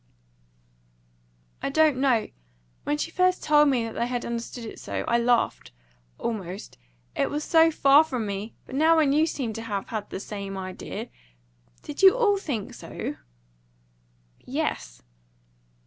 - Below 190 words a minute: Yes, average, 150 wpm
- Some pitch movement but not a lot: No, wide, 5.8 semitones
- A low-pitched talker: No, high, 245 Hz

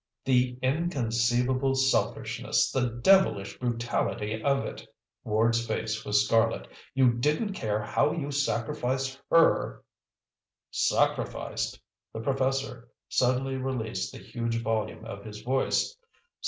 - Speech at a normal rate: No, slow, 115 wpm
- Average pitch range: Yes, average, 3.0 semitones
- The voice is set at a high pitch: No, low, 125 Hz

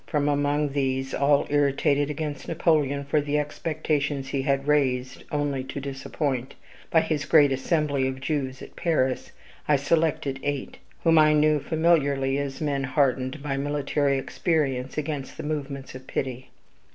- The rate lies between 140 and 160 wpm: Yes, average, 150 wpm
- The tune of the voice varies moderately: No, narrow, 1.9 semitones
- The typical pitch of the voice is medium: Yes, medium, 145 Hz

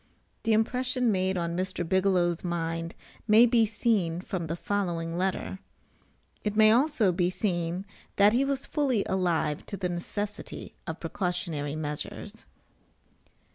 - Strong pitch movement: No, average, 4.1 semitones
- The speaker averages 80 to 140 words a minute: Yes, slow, 135 wpm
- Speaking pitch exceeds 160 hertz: Yes, medium, 185 Hz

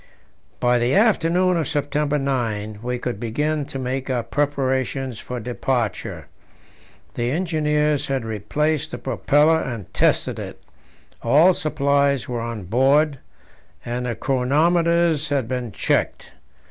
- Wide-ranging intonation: No, average, 3.7 semitones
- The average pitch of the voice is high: No, low, 135 Hz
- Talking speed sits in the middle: No, slow, 125 wpm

